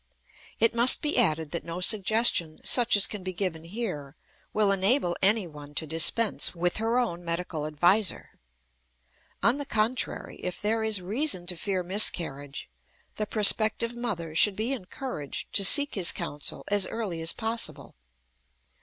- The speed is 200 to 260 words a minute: No, average, 150 wpm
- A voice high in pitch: Yes, high, 195 Hz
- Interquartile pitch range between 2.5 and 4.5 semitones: No, average, 5.0 semitones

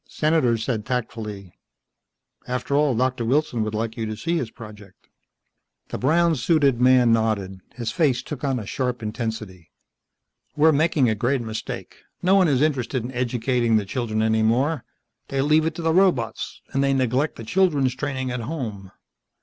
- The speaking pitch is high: No, low, 125 Hz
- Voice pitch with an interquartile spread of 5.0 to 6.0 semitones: No, average, 4.5 semitones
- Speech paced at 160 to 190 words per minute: Yes, average, 170 wpm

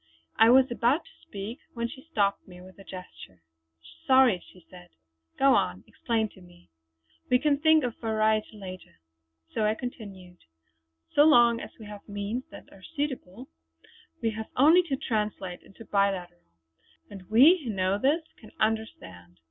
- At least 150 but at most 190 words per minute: Yes, average, 165 wpm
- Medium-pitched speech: No, high, 215 Hz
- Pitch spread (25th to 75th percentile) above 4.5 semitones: Yes, average, 4.9 semitones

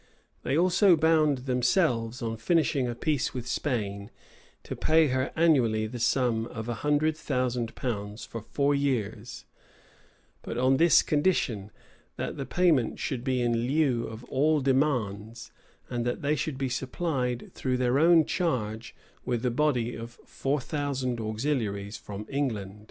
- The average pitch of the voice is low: Yes, low, 125 Hz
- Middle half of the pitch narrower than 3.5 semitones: No, average, 4.1 semitones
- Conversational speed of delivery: Yes, average, 150 wpm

